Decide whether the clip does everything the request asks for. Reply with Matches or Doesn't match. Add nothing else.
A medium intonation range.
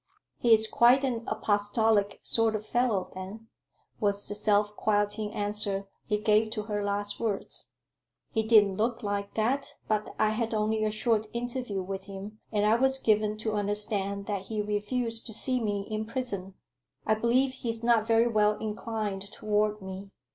Doesn't match